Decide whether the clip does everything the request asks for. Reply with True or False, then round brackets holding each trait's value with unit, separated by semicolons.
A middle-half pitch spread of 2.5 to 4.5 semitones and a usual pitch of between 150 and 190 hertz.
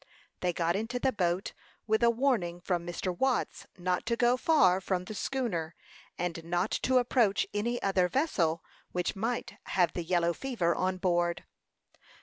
False (5.2 semitones; 185 Hz)